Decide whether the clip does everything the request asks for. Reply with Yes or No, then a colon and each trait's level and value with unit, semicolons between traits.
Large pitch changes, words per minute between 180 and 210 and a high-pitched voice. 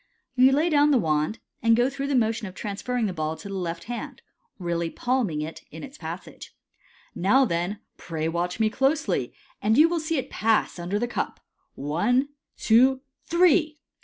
Yes: wide, 7.4 semitones; average, 185 wpm; high, 225 Hz